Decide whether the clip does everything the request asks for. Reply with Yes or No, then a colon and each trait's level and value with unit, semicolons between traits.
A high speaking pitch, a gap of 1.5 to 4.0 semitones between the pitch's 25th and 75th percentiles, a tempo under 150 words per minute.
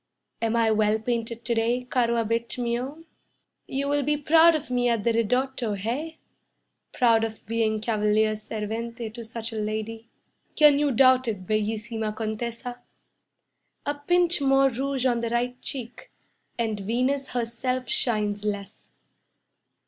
Yes: high, 235 Hz; average, 2.9 semitones; average, 140 wpm